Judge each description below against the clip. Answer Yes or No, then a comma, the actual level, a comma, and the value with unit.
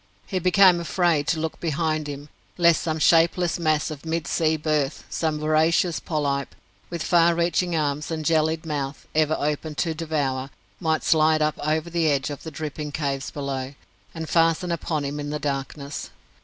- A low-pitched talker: No, medium, 155 Hz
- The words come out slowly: No, average, 170 wpm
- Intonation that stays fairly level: Yes, narrow, 2.2 semitones